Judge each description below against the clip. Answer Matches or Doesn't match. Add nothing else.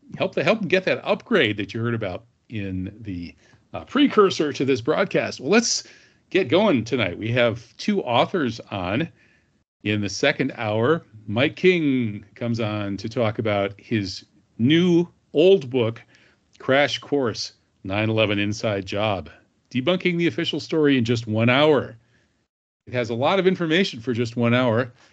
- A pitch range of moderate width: Doesn't match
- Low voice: Matches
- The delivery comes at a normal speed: Matches